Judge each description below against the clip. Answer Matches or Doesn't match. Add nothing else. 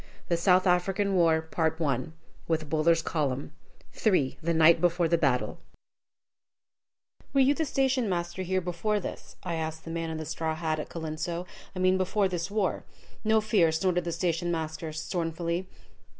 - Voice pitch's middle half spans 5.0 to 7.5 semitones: Doesn't match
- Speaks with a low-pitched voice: Doesn't match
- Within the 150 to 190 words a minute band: Doesn't match